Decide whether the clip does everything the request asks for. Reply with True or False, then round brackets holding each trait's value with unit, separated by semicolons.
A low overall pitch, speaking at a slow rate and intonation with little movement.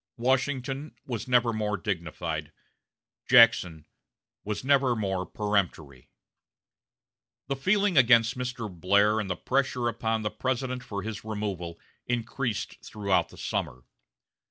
False (110 Hz; 115 wpm; 3.9 semitones)